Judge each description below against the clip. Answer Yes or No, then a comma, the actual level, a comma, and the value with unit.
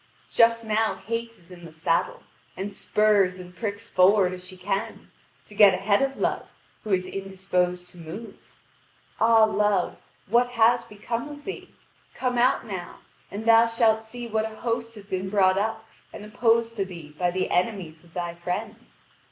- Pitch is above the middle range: Yes, high, 205 Hz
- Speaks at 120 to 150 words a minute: No, average, 175 wpm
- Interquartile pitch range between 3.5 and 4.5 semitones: Yes, average, 3.8 semitones